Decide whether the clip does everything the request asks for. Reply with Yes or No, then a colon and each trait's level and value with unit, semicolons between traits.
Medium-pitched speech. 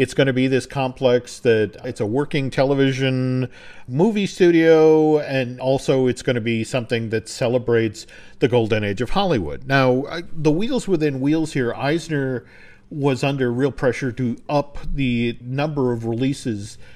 No: low, 130 Hz